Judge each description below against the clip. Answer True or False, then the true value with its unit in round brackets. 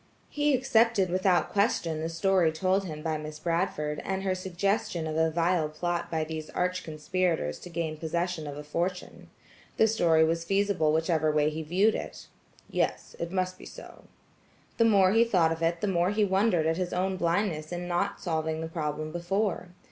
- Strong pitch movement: False (3.2 semitones)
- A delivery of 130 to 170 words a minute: False (185 wpm)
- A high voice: False (175 Hz)